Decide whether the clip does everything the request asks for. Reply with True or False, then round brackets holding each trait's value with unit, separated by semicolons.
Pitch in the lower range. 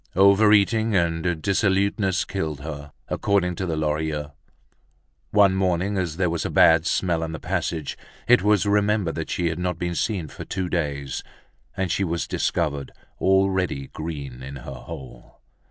True (85 Hz)